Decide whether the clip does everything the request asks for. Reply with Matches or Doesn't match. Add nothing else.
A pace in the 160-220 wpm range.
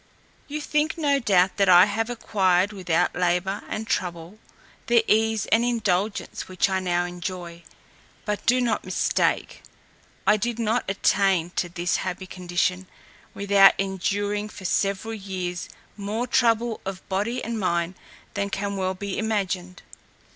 Doesn't match